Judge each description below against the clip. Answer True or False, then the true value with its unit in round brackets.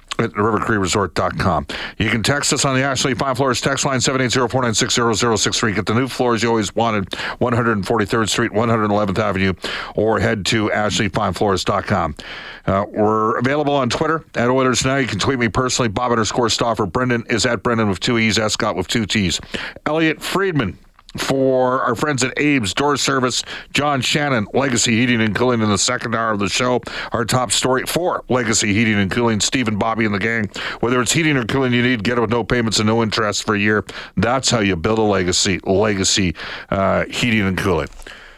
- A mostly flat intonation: False (3.3 semitones)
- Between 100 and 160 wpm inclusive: False (190 wpm)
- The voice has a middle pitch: False (115 Hz)